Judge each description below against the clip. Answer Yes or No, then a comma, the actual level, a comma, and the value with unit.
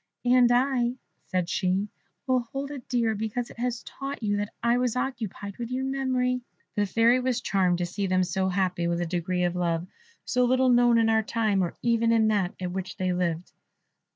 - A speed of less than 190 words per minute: No, fast, 205 wpm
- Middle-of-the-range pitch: No, high, 220 Hz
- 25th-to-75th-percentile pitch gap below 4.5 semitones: No, average, 5.0 semitones